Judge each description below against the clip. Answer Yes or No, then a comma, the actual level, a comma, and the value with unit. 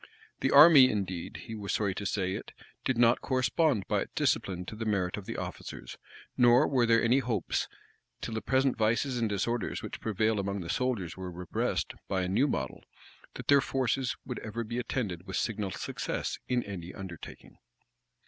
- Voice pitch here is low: Yes, low, 110 Hz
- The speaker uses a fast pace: No, average, 185 wpm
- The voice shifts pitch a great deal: No, average, 4.6 semitones